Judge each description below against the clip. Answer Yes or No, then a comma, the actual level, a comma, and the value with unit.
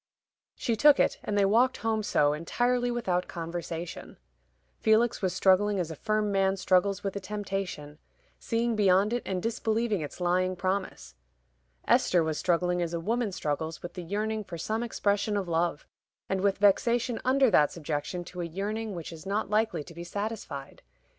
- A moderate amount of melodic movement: Yes, average, 3.9 semitones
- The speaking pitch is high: Yes, high, 195 Hz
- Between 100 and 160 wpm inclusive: No, average, 175 wpm